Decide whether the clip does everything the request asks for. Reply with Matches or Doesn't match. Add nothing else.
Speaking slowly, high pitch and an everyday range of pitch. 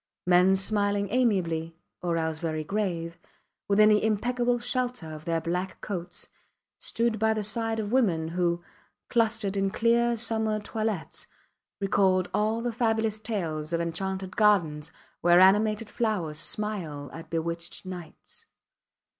Matches